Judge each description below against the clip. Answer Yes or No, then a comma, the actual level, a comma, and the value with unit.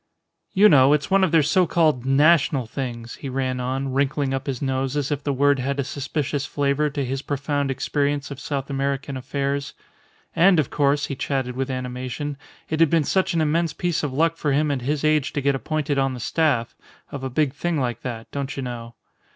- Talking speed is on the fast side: Yes, fast, 215 wpm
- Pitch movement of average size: No, narrow, 2.1 semitones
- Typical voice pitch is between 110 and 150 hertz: Yes, medium, 140 Hz